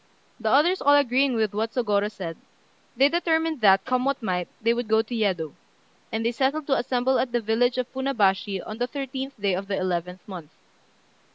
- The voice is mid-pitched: No, high, 235 Hz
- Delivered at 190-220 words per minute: Yes, average, 195 wpm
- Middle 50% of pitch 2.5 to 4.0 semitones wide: No, average, 4.7 semitones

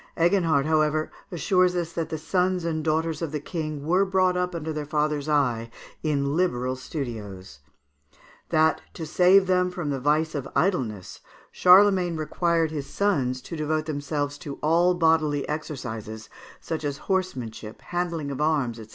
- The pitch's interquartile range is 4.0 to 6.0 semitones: No, average, 3.6 semitones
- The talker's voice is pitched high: No, medium, 155 Hz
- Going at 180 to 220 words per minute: No, average, 155 wpm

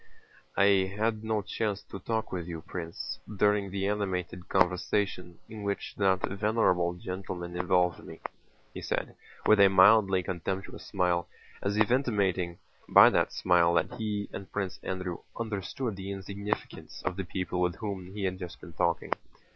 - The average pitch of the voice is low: Yes, very low, 95 Hz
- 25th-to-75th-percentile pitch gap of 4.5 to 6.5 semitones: No, narrow, 2.4 semitones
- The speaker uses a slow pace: No, average, 155 wpm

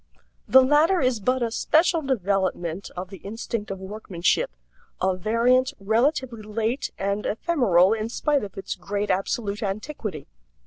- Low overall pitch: No, high, 215 Hz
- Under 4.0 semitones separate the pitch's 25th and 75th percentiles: No, average, 4.8 semitones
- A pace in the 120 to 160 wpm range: Yes, average, 140 wpm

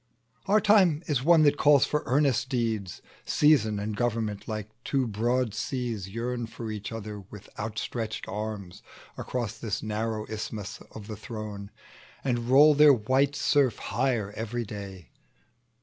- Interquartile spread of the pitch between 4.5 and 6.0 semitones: No, average, 3.9 semitones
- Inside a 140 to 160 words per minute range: Yes, average, 145 wpm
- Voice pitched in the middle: No, low, 115 Hz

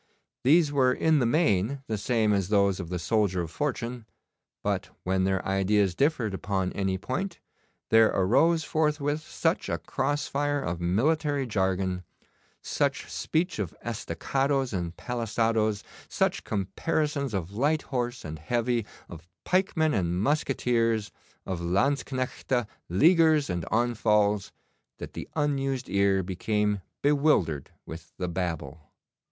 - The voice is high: No, low, 110 Hz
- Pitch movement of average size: No, wide, 6.7 semitones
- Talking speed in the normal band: No, slow, 130 wpm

